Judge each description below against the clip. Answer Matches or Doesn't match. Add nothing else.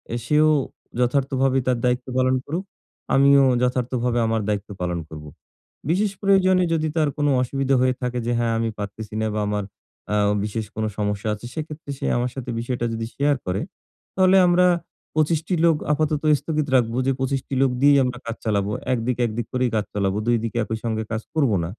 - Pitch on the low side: Matches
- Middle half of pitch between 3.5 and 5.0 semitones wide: Matches